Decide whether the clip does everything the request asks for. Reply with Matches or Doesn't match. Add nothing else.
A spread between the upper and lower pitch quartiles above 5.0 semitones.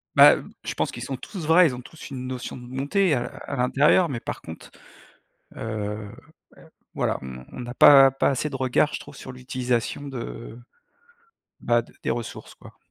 Doesn't match